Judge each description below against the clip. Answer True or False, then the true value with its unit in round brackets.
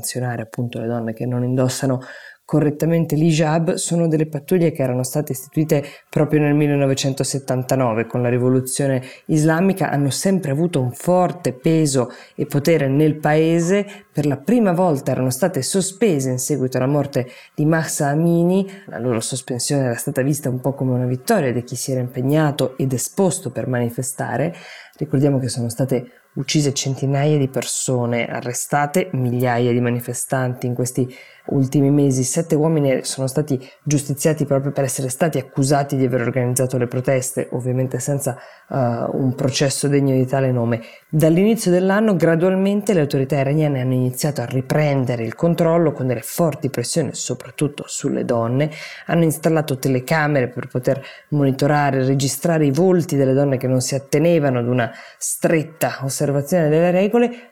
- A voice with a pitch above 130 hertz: True (140 Hz)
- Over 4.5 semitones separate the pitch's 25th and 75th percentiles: False (3.5 semitones)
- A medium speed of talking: True (155 wpm)